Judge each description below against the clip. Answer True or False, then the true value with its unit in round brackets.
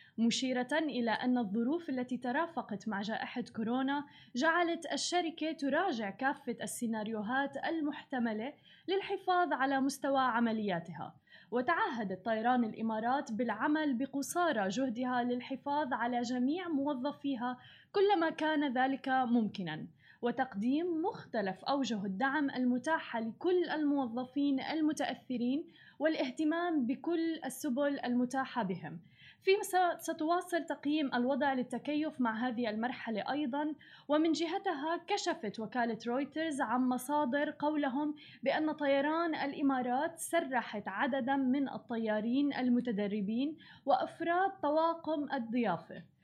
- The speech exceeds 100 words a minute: False (95 wpm)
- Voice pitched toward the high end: True (270 Hz)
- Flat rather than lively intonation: False (4.2 semitones)